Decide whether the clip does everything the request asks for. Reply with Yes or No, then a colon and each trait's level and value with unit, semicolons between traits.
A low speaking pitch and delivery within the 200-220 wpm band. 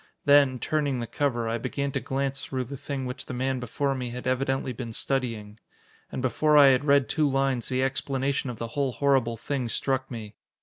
Yes: low, 130 Hz; fast, 205 wpm